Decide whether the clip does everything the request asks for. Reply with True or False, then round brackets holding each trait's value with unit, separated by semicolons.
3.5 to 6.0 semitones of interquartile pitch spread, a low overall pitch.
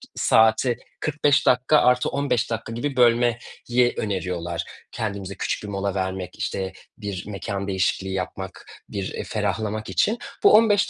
True (4.4 semitones; 105 Hz)